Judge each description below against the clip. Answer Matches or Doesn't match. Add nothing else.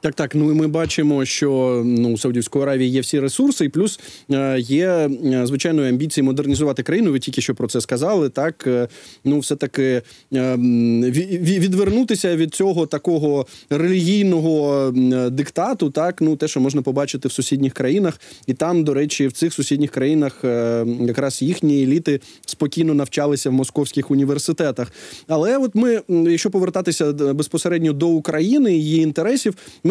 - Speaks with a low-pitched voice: Doesn't match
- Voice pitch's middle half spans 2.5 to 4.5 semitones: Matches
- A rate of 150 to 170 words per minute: Matches